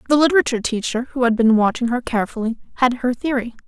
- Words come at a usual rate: Yes, average, 195 wpm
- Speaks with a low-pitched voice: No, high, 245 Hz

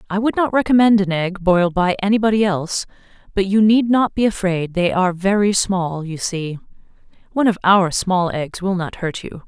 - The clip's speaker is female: Yes, female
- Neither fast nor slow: Yes, average, 195 wpm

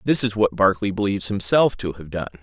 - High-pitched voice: No, low, 100 Hz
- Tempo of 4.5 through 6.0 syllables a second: No, 6.3 syllables/s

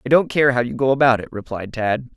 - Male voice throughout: Yes, male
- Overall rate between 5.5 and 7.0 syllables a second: Yes, 6.0 syllables/s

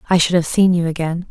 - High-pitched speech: No, medium, 170 Hz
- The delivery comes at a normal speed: No, fast, 275 wpm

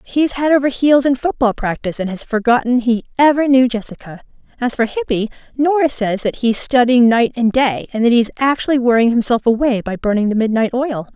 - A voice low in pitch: No, high, 245 Hz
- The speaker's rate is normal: No, fast, 210 wpm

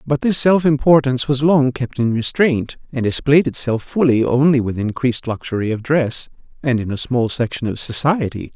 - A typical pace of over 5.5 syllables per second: No, 5.1 syllables/s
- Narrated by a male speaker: Yes, male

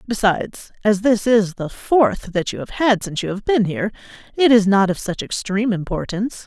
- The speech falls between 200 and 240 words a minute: Yes, fast, 205 wpm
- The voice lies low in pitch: No, high, 210 Hz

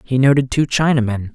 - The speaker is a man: Yes, male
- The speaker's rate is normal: Yes, average, 180 wpm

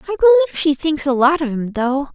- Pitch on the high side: Yes, very high, 305 Hz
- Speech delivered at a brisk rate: Yes, fast, 250 wpm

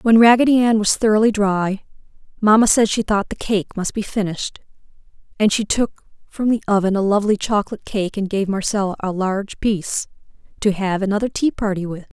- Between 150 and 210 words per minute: Yes, average, 180 wpm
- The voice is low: No, high, 205 Hz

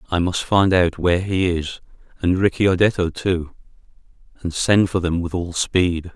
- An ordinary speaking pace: Yes, average, 165 wpm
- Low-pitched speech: Yes, very low, 90 Hz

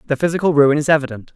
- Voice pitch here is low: No, medium, 145 Hz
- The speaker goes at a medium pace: No, fast, 220 wpm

